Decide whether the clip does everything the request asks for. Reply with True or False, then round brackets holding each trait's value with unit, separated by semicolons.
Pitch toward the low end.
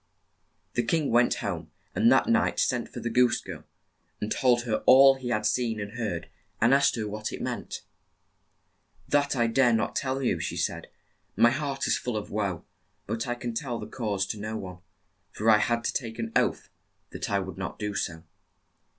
True (115 Hz)